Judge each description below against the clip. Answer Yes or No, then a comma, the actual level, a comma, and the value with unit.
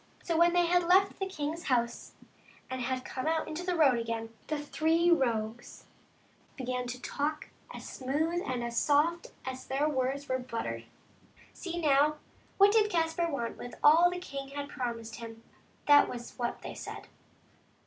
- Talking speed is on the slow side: No, average, 175 wpm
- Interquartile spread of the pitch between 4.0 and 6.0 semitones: Yes, average, 5.1 semitones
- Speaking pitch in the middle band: No, very high, 285 Hz